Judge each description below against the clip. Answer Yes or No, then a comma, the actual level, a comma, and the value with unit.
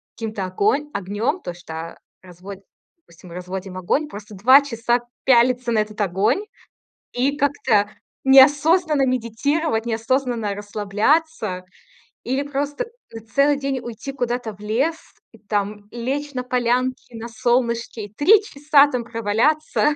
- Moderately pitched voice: No, high, 240 Hz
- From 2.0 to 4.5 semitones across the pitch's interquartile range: No, average, 5.1 semitones